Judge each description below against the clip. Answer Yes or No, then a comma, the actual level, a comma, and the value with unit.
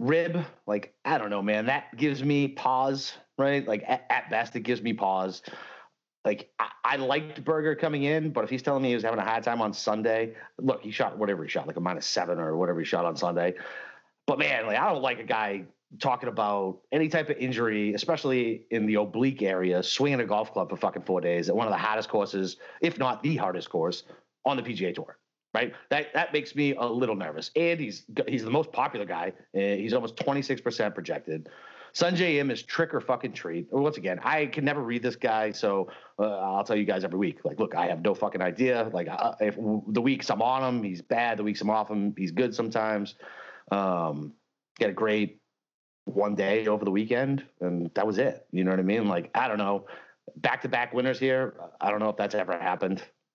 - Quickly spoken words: Yes, fast, 230 wpm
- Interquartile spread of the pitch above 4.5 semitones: Yes, average, 5.2 semitones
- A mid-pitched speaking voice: No, low, 115 Hz